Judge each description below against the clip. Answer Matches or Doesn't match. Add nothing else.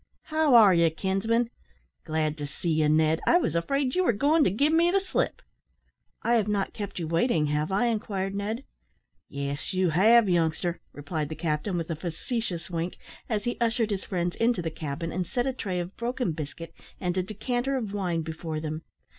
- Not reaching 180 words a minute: Doesn't match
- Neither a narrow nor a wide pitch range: Doesn't match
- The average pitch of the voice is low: Doesn't match